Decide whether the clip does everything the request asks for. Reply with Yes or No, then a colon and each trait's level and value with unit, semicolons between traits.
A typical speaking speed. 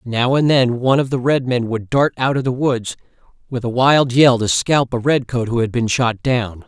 No: fast, 250 wpm